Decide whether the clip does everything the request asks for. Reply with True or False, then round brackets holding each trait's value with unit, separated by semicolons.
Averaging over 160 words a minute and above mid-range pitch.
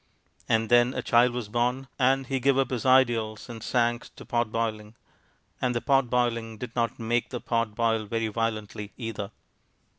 False (180 wpm; 120 Hz)